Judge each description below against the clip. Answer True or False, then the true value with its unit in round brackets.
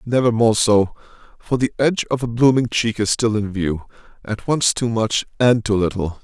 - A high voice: False (110 Hz)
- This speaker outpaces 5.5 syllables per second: False (4.9 syllables/s)